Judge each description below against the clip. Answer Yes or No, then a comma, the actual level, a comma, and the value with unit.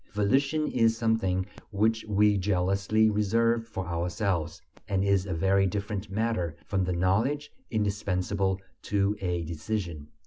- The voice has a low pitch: Yes, low, 100 Hz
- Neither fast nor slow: No, slow, 130 wpm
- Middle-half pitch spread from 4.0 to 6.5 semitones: No, average, 3.0 semitones